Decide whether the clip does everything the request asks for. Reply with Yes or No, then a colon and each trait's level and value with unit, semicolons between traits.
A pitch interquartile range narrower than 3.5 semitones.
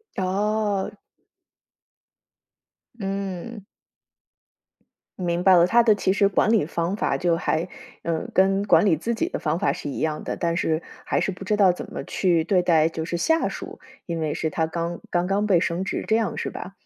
Yes: average, 3.1 semitones